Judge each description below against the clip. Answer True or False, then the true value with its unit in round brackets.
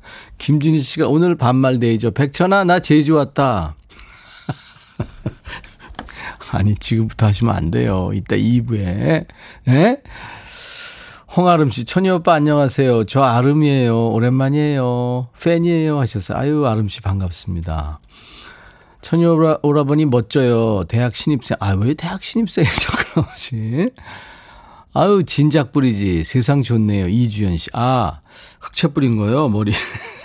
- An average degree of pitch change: False (6.1 semitones)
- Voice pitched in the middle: False (130 Hz)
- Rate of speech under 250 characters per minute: False (260 characters per minute)